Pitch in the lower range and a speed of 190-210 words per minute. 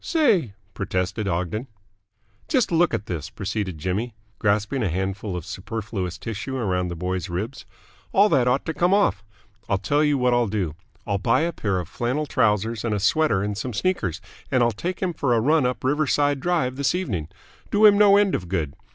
Yes: low, 115 Hz; average, 195 wpm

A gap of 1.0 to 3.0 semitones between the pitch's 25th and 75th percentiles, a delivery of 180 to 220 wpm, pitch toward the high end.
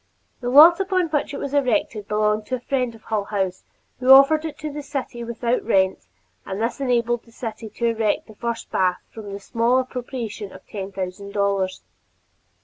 No: average, 4.3 semitones; average, 195 wpm; high, 235 Hz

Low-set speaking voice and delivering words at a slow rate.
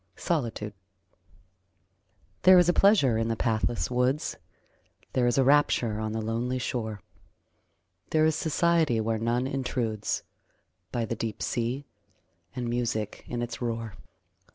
Yes: low, 120 Hz; slow, 130 wpm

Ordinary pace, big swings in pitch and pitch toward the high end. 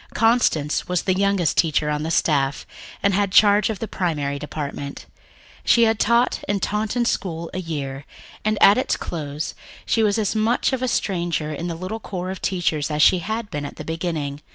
No: average, 195 wpm; wide, 5.7 semitones; medium, 180 Hz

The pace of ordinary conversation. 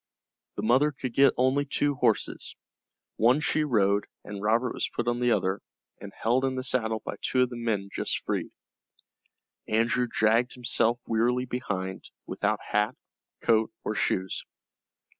Yes: average, 155 wpm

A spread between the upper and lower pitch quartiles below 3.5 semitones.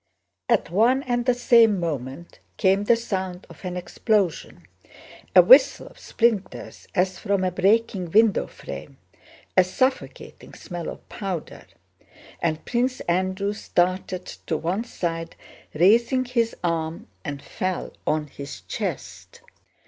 No: average, 4.9 semitones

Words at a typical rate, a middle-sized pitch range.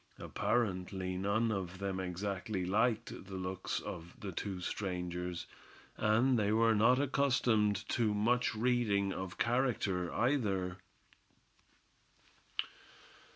No: slow, 105 wpm; average, 3.9 semitones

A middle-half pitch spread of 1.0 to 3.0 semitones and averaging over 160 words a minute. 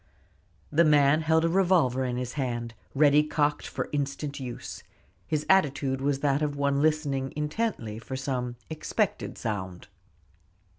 No: average, 2.7 semitones; average, 140 wpm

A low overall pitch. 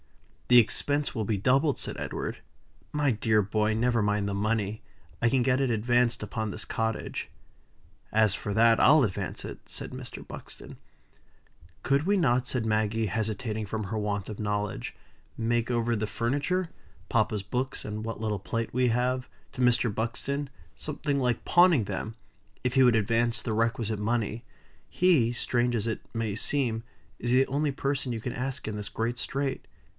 Yes: low, 115 Hz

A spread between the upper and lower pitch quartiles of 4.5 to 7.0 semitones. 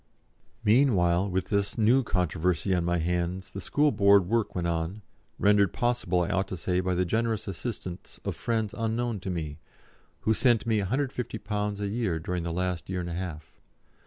No: average, 3.9 semitones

